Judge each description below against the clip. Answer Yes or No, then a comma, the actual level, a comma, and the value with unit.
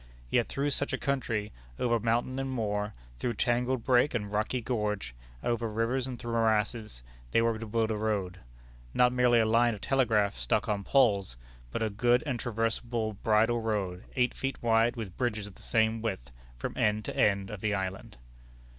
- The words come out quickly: No, average, 185 wpm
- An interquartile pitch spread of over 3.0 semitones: No, narrow, 2.5 semitones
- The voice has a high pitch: No, low, 115 Hz